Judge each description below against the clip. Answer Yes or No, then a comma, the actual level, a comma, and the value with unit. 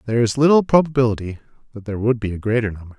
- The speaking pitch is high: No, low, 115 Hz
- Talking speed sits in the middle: No, fast, 220 wpm